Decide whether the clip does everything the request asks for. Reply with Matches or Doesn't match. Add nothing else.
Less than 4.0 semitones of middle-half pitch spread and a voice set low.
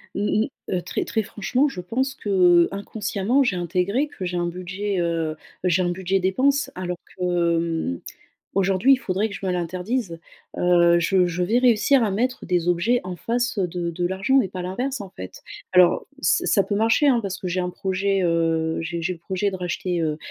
Doesn't match